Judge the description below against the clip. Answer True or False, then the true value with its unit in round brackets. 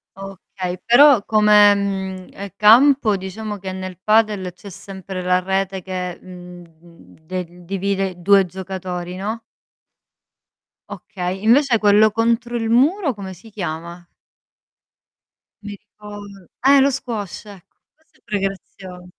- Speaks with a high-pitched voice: True (195 Hz)